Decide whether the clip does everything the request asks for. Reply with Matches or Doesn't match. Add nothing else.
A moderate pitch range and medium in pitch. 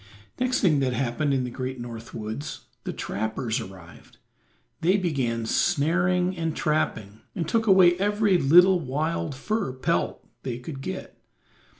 Doesn't match